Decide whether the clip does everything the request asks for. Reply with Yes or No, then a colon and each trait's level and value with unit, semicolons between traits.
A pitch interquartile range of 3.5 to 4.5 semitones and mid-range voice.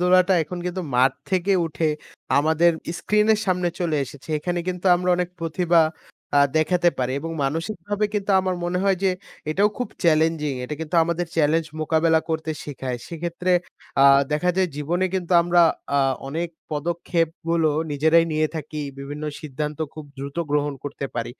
No: average, 2.9 semitones; medium, 165 Hz